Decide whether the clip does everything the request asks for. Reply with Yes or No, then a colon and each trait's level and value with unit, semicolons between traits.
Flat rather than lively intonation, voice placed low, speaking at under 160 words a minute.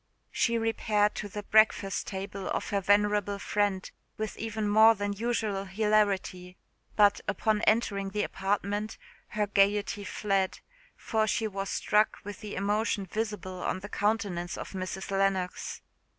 No: narrow, 1.6 semitones; high, 205 Hz; average, 140 wpm